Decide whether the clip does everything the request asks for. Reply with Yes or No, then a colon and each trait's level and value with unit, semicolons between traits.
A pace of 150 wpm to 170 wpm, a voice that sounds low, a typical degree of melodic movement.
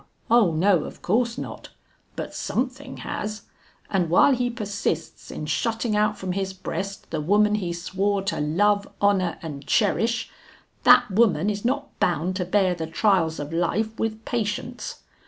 No: average, 155 wpm; high, 200 Hz; average, 4.0 semitones